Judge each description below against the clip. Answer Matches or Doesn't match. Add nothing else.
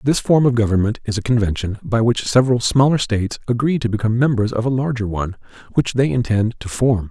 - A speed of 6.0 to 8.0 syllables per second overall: Matches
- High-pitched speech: Doesn't match